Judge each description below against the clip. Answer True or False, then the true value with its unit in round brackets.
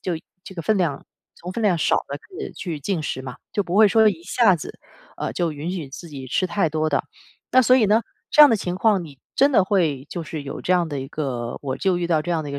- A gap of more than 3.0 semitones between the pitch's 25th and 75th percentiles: True (5.2 semitones)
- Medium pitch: True (175 Hz)